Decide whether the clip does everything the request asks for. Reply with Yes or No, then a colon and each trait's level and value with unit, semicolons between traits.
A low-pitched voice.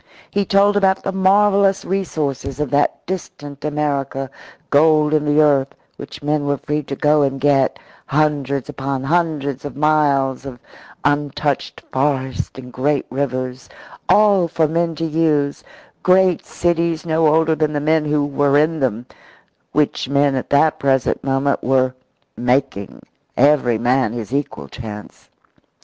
No: medium, 145 Hz